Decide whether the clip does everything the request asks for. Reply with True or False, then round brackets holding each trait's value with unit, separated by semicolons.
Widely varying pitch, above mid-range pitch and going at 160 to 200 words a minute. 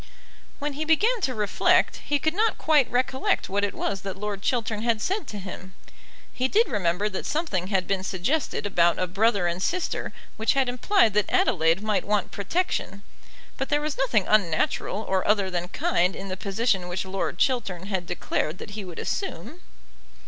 True (6.0 semitones; 205 Hz; 185 wpm)